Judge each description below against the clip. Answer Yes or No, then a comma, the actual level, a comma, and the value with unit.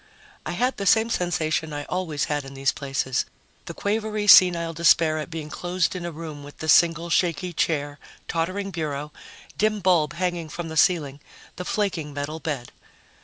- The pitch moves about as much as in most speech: Yes, average, 3.4 semitones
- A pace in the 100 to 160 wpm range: No, average, 170 wpm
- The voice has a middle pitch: Yes, medium, 165 Hz